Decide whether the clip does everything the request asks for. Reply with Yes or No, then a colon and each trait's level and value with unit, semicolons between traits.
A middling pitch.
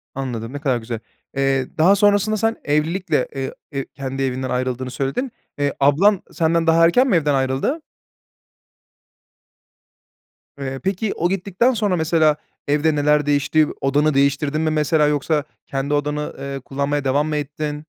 Yes: medium, 150 Hz